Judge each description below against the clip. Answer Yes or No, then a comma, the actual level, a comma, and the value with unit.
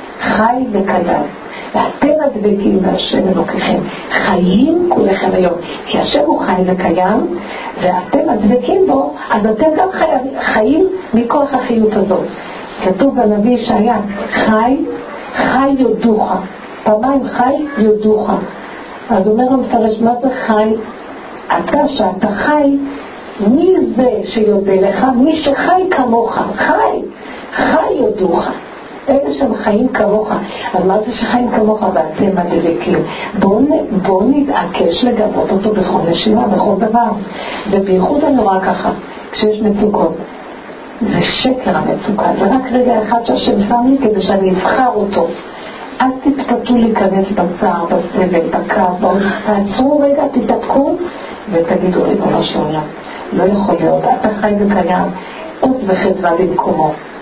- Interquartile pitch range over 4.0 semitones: Yes, average, 4.8 semitones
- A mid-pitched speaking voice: No, high, 220 Hz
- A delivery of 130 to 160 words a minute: No, average, 120 wpm